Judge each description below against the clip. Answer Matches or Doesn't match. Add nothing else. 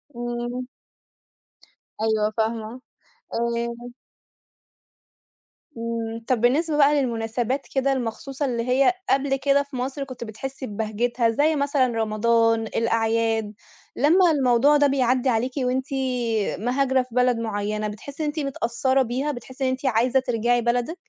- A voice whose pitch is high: Matches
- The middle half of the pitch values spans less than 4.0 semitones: Matches